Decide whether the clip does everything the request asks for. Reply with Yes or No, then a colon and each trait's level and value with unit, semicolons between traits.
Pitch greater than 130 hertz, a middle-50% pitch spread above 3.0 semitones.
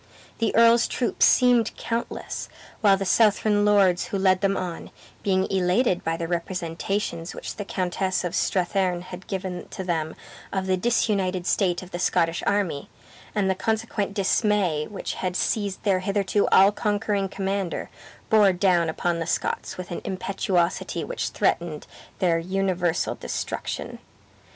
No: high, 190 Hz; narrow, 2.4 semitones